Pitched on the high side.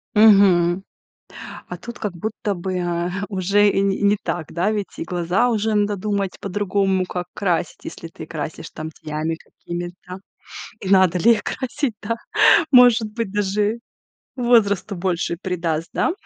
Yes: high, 195 Hz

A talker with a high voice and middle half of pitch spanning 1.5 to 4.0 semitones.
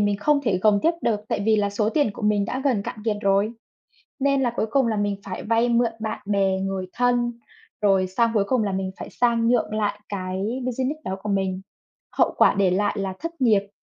Yes: high, 210 Hz; average, 3.4 semitones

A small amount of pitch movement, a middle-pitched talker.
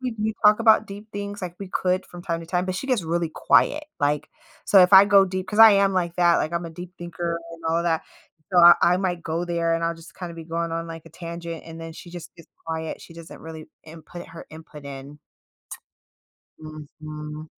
Yes: narrow, 2.2 semitones; medium, 170 Hz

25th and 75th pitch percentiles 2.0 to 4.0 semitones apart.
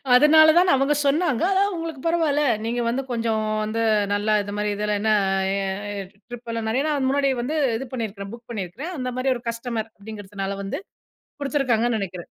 No: average, 4.7 semitones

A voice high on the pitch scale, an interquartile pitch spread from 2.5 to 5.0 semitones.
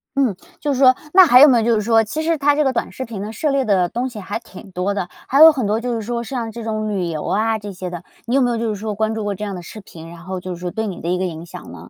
Yes: high, 220 Hz; average, 4.7 semitones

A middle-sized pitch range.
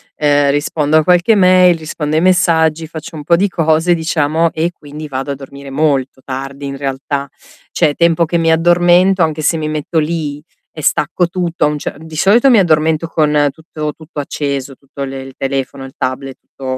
Yes: average, 3.1 semitones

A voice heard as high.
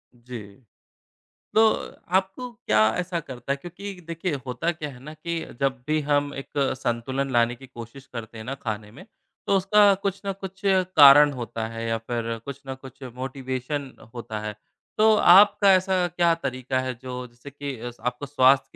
No: low, 135 Hz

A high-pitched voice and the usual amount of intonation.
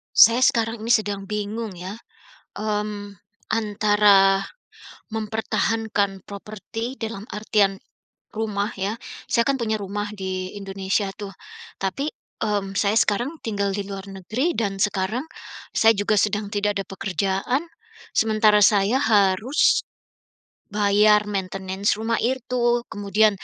No: high, 210 Hz; narrow, 2.1 semitones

